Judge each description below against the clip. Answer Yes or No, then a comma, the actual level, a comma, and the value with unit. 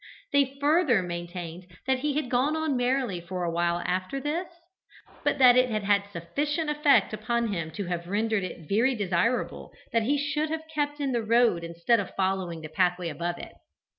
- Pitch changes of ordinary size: No, wide, 7.7 semitones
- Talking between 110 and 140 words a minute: No, average, 190 wpm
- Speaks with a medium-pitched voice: No, high, 220 Hz